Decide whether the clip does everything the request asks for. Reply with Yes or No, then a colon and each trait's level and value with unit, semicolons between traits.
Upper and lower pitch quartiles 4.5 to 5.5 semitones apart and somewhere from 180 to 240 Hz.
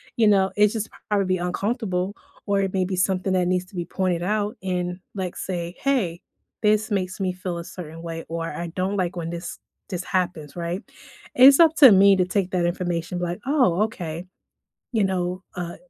No: narrow, 2.4 semitones; medium, 185 Hz